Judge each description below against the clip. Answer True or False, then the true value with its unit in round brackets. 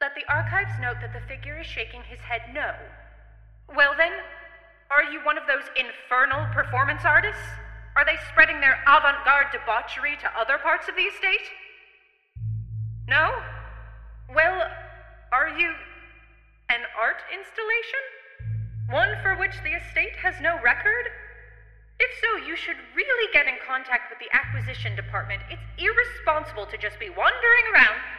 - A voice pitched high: True (310 Hz)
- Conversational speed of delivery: True (145 wpm)